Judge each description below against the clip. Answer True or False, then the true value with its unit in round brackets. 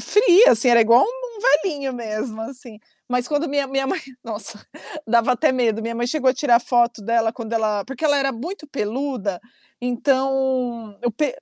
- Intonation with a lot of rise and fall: False (3.4 semitones)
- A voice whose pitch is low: False (250 Hz)